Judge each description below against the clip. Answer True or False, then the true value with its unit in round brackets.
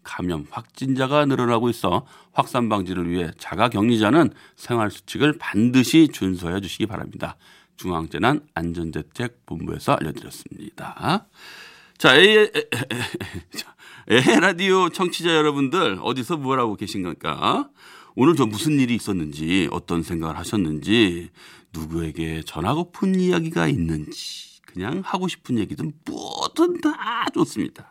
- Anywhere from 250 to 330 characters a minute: True (290 characters per minute)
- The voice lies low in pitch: True (115 Hz)